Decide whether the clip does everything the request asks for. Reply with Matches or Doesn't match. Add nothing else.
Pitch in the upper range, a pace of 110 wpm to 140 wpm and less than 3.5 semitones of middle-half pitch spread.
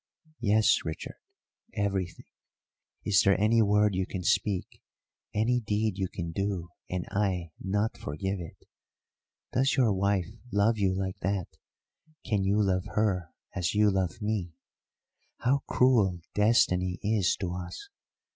Doesn't match